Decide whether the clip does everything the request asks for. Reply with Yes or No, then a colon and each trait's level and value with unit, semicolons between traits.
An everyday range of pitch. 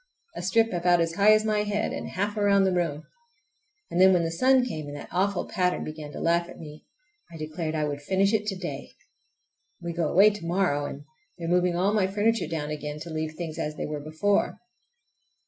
Yes: average, 4.3 semitones